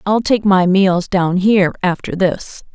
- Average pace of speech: Yes, average, 175 wpm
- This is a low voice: No, high, 190 Hz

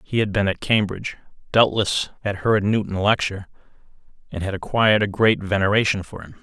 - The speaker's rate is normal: Yes, average, 170 wpm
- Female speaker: No, male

